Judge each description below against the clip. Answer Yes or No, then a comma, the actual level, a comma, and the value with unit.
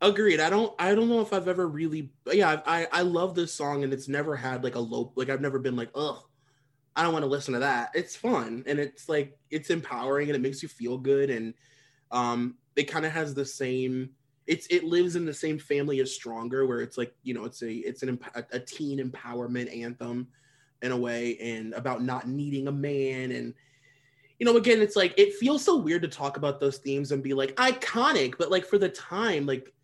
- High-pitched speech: No, medium, 140 Hz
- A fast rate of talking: Yes, fast, 230 wpm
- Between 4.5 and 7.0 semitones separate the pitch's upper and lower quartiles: No, average, 3.8 semitones